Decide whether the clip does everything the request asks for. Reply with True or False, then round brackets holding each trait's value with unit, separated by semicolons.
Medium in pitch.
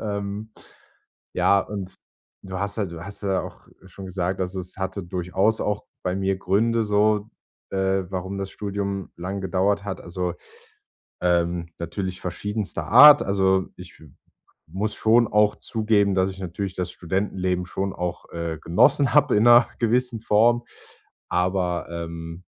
False (95 Hz)